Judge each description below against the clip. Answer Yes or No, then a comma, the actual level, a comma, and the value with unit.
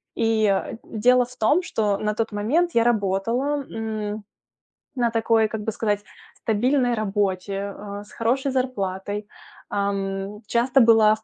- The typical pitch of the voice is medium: No, high, 220 Hz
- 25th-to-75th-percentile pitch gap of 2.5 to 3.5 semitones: Yes, average, 2.8 semitones